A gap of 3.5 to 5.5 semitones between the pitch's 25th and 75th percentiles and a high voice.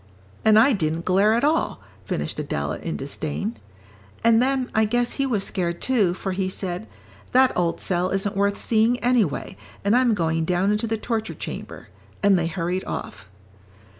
Yes: average, 4.7 semitones; high, 200 Hz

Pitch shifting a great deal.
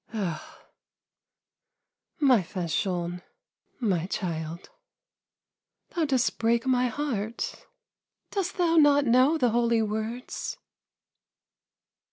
Yes: wide, 6.1 semitones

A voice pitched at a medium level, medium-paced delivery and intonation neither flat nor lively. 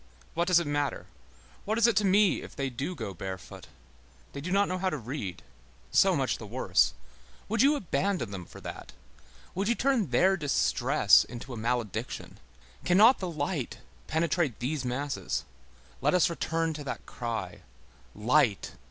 No: medium, 150 Hz; average, 165 wpm; wide, 7.2 semitones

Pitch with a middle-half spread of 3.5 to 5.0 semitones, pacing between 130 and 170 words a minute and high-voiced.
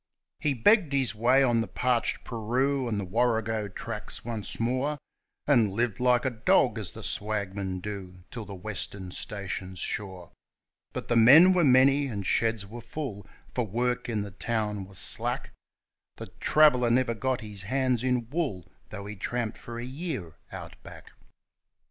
No: average, 4.0 semitones; average, 160 wpm; low, 115 Hz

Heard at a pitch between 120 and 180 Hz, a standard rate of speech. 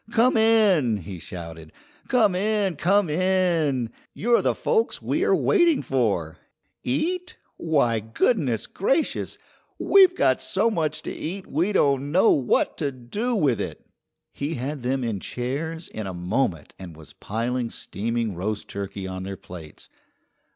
Yes: medium, 140 Hz; average, 150 wpm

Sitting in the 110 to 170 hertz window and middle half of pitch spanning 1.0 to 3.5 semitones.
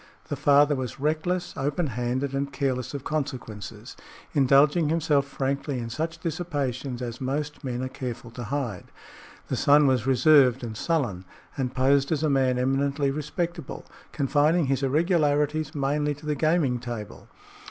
Yes: medium, 140 Hz; average, 2.7 semitones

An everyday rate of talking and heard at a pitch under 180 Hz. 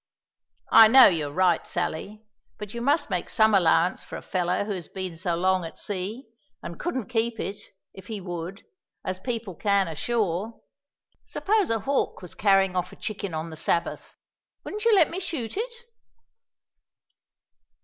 No: average, 165 wpm; high, 200 Hz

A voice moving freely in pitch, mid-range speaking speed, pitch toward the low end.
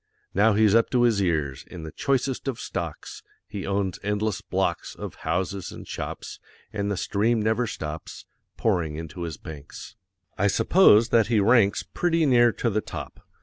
No: average, 4.4 semitones; average, 170 wpm; low, 105 Hz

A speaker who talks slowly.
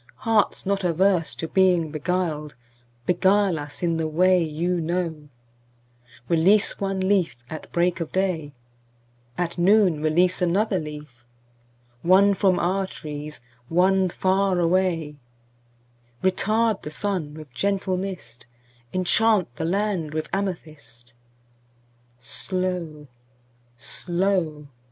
Yes: slow, 90 wpm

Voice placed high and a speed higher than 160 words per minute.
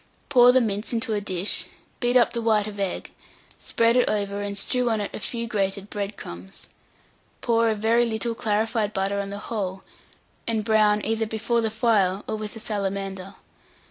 Yes: high, 215 Hz; average, 185 wpm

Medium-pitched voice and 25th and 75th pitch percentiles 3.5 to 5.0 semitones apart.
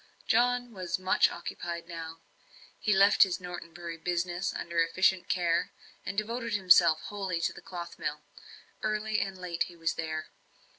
No: medium, 180 Hz; average, 2.8 semitones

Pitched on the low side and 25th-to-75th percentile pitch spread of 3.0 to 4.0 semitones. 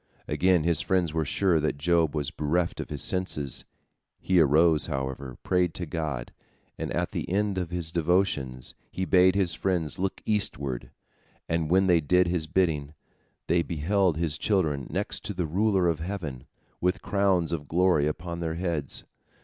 Yes: very low, 85 Hz; average, 3.3 semitones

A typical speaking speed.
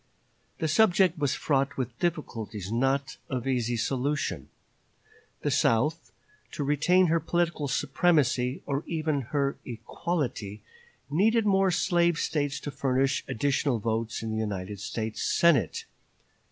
No: slow, 125 wpm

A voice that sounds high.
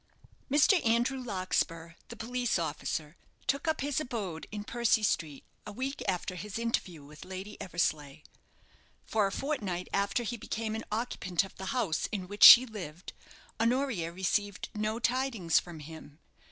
Yes: high, 205 Hz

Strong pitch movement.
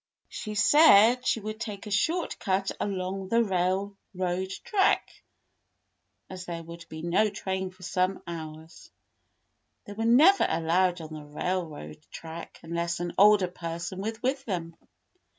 No: average, 3.7 semitones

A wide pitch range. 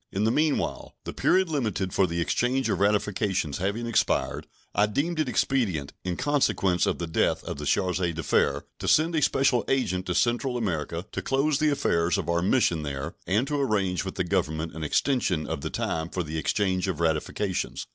Yes: wide, 7.4 semitones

